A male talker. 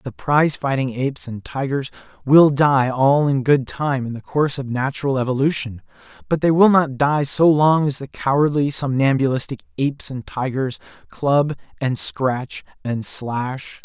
Yes: male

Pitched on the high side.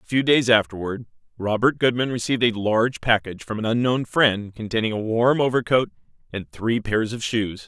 No: low, 115 Hz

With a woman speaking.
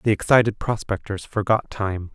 No: male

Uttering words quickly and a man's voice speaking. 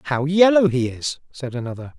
No: average, 180 wpm; male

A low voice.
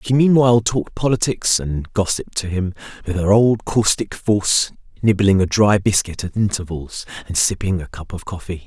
Yes: low, 100 Hz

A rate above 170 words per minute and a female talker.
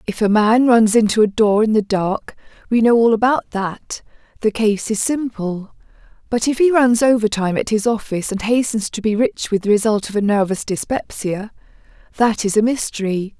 Yes: average, 180 wpm; female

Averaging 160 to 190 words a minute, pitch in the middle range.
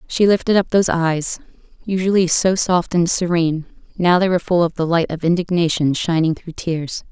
Yes: average, 185 wpm; medium, 175 Hz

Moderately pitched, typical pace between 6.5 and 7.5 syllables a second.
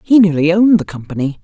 Yes: medium, 175 Hz; 6.8 syllables/s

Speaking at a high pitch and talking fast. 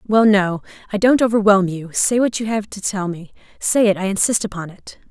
Yes: high, 205 Hz; fast, 210 wpm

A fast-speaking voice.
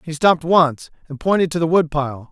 Yes: fast, 235 wpm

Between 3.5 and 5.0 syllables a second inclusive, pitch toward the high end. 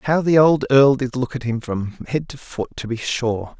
No: 4.7 syllables/s; low, 130 Hz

